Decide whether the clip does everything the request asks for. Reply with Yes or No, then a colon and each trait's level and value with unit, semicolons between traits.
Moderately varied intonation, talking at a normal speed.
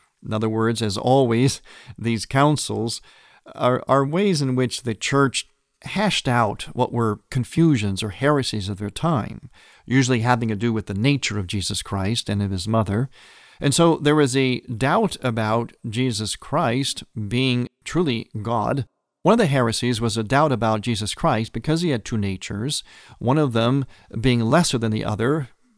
Yes: average, 3.8 semitones; average, 170 wpm